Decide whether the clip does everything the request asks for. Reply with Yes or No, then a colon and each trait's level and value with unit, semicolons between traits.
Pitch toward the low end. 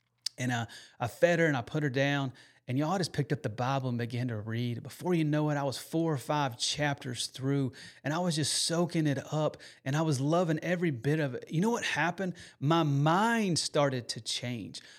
No: medium, 145 Hz